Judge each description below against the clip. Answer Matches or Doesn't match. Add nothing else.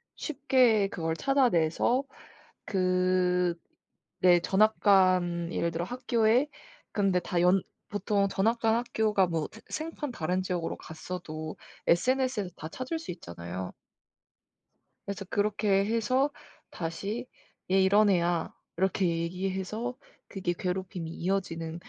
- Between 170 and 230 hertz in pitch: Matches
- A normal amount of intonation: Matches